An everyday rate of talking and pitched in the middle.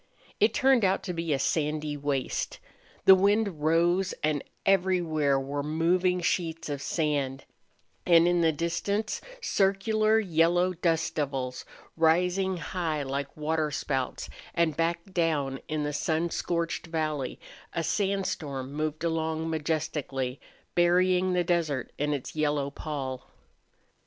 No: slow, 125 wpm; medium, 160 Hz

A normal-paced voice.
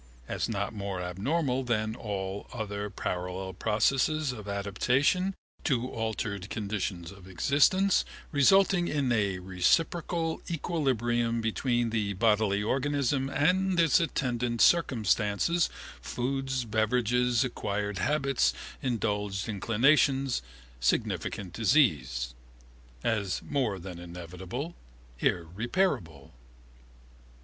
No: slow, 90 wpm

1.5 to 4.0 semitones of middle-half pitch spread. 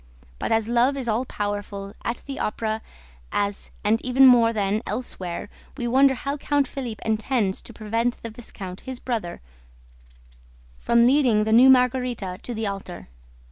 Yes: average, 3.3 semitones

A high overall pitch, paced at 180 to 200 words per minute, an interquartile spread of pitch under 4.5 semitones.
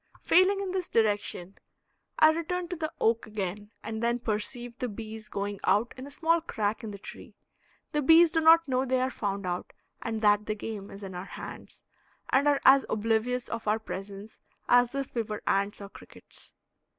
No: high, 225 Hz; average, 195 wpm; average, 5.1 semitones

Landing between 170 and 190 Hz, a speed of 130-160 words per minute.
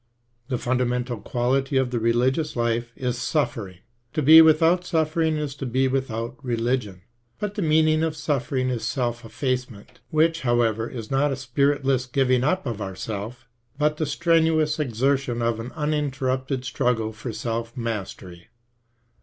No: low, 130 Hz; average, 150 wpm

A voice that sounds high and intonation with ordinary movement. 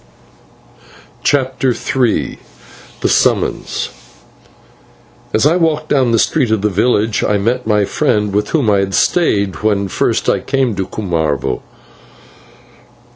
No: low, 110 Hz; average, 4.7 semitones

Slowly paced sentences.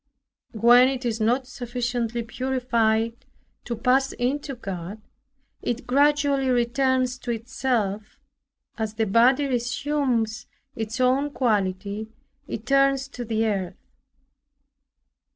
Yes: slow, 105 wpm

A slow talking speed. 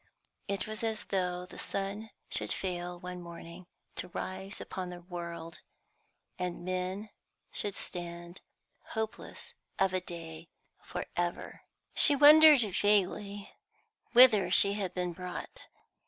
Yes: slow, 120 wpm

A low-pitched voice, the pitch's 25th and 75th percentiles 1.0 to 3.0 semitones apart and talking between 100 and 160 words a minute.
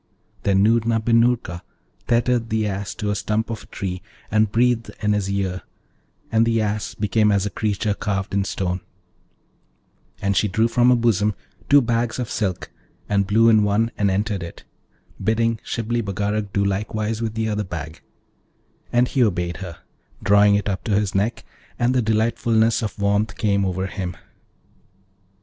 No: low, 105 Hz; narrow, 2.4 semitones; average, 170 wpm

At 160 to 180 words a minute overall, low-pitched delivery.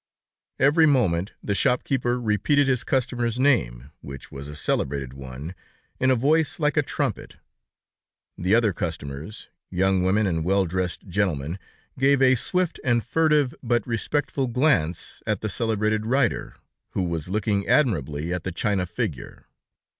No: average, 145 wpm; low, 105 Hz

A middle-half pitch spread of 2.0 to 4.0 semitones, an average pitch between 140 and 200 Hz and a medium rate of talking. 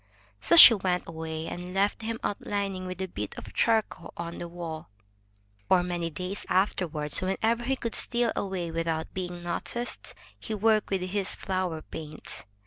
Yes: average, 3.5 semitones; medium, 185 Hz; average, 165 wpm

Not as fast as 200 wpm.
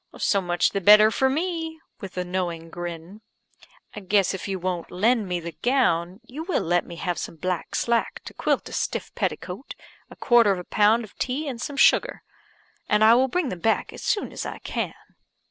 No: fast, 205 wpm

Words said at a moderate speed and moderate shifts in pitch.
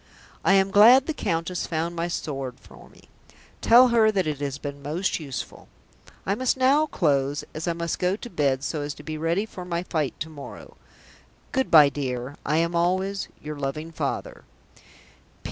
Yes: average, 180 wpm; average, 5.0 semitones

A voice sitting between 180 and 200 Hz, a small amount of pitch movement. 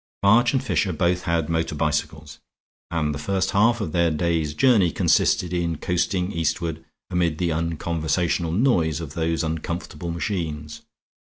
No: very low, 85 Hz; narrow, 2.2 semitones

